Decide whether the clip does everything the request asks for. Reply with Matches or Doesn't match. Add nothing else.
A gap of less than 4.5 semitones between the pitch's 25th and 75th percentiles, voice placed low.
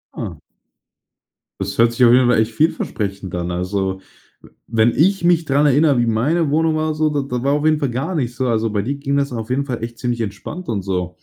Doesn't match